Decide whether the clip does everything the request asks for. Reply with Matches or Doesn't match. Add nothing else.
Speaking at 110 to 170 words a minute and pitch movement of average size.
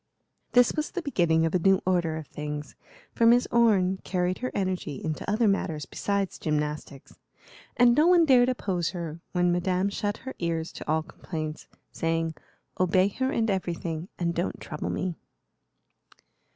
Matches